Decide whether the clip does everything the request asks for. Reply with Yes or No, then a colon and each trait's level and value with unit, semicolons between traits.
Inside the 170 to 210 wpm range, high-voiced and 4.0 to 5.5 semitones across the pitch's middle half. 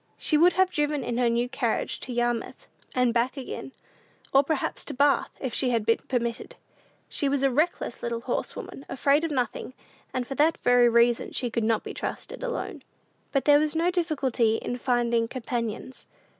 No: average, 180 wpm; very high, 255 Hz; average, 3.6 semitones